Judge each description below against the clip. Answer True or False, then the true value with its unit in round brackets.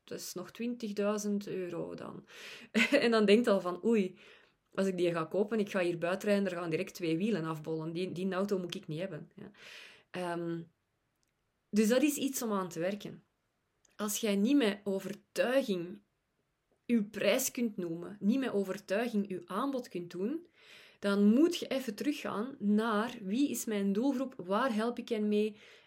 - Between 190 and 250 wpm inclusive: False (180 wpm)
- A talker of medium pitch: False (205 Hz)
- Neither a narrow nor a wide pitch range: True (3.8 semitones)